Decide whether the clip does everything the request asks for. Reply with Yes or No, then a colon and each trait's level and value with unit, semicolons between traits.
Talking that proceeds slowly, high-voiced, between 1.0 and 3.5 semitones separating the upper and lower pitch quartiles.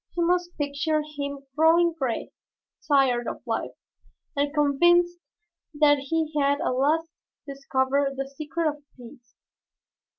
Yes: slow, 125 wpm; very high, 290 Hz; average, 2.9 semitones